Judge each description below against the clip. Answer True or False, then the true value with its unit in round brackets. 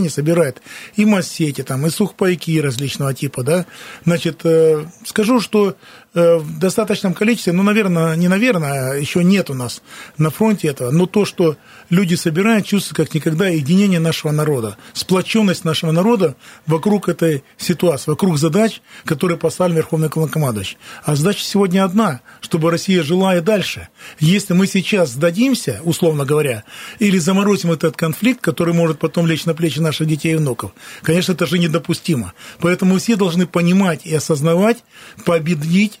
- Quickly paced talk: False (150 wpm)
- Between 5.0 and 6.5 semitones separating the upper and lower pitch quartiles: False (3.5 semitones)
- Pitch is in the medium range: True (170 Hz)